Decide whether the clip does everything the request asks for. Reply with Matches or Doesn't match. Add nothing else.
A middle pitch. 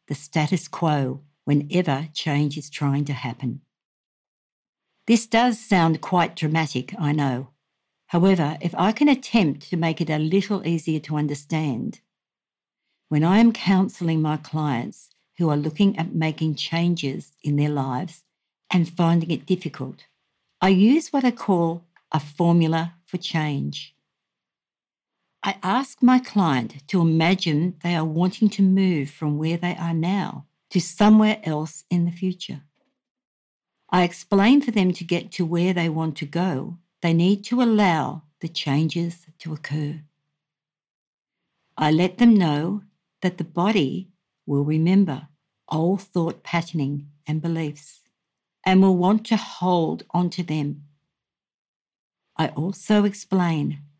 Matches